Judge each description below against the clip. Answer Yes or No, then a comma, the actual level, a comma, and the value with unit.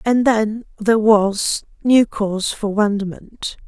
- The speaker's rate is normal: No, slow, 130 wpm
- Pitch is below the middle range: No, high, 215 Hz